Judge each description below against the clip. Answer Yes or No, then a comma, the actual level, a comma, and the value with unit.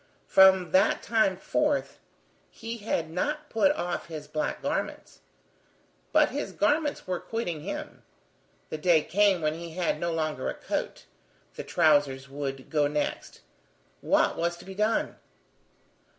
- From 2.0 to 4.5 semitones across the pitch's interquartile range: No, average, 5.2 semitones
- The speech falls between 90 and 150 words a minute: Yes, average, 140 wpm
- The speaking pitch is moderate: Yes, medium, 175 Hz